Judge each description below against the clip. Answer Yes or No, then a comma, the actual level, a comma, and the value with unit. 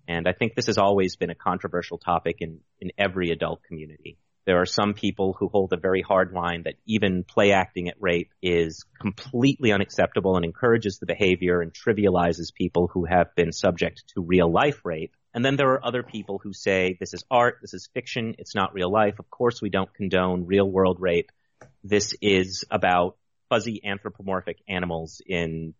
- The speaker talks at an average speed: Yes, average, 190 wpm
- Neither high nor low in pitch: No, very low, 95 Hz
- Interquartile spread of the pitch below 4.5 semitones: Yes, average, 2.7 semitones